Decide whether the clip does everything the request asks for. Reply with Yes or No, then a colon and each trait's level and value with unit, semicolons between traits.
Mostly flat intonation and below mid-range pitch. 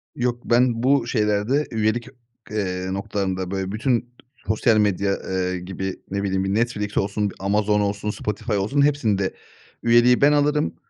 No: average, 3.4 semitones; low, 105 Hz